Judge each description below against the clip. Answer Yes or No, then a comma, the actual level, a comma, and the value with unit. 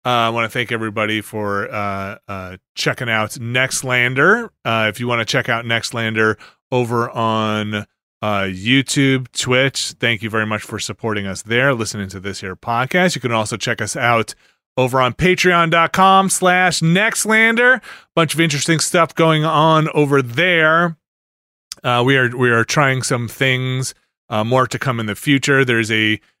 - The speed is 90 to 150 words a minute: No, average, 170 wpm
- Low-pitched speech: Yes, low, 125 Hz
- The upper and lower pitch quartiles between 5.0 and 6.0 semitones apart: Yes, wide, 5.4 semitones